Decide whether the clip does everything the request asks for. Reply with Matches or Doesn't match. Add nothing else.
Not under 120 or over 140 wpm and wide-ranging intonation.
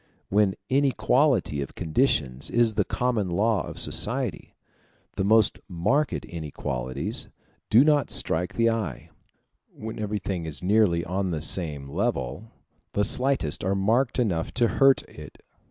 Matches